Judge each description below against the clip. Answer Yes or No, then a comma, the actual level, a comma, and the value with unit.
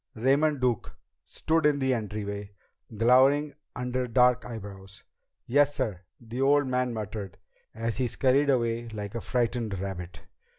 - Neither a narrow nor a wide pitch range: Yes, average, 3.9 semitones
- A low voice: Yes, low, 120 Hz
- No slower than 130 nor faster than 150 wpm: Yes, slow, 135 wpm